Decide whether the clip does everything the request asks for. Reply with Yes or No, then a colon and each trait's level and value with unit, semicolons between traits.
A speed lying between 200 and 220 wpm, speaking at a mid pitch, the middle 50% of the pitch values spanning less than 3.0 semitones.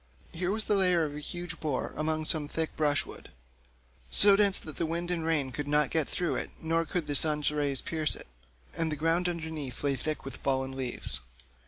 Yes: fast, 205 wpm; medium, 155 Hz; narrow, 2.5 semitones